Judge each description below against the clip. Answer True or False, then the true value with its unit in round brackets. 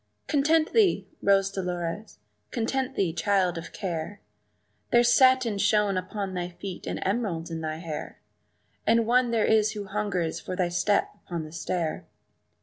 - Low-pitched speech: False (200 Hz)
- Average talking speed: True (150 wpm)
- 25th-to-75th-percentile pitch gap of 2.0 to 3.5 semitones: False (4.3 semitones)